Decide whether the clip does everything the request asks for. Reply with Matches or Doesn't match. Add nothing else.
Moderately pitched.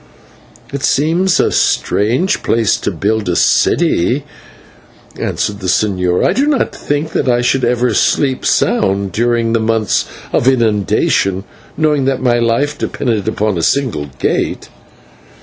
Doesn't match